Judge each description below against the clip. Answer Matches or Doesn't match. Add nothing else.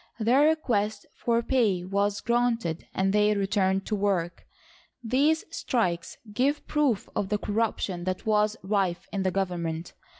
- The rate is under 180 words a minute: Matches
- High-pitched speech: Matches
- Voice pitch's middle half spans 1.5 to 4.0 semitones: Matches